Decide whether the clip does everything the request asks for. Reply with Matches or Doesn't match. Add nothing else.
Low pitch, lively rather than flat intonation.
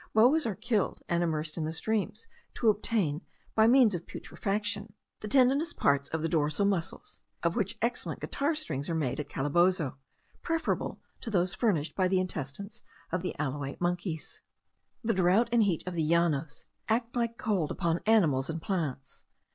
Doesn't match